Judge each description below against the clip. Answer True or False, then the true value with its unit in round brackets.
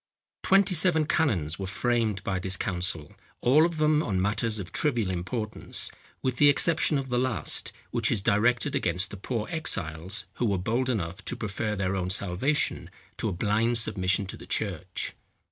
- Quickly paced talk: False (175 wpm)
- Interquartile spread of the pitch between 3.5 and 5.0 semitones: False (5.6 semitones)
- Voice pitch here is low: True (105 Hz)